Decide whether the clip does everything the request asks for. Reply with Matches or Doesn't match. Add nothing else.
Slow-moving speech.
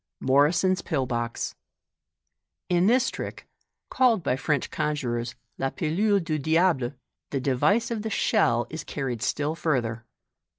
Doesn't match